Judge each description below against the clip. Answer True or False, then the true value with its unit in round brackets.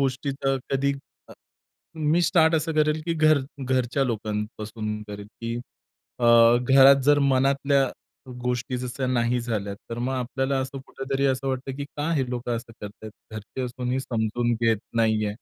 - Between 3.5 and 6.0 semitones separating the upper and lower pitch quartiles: False (2.9 semitones)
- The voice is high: False (130 Hz)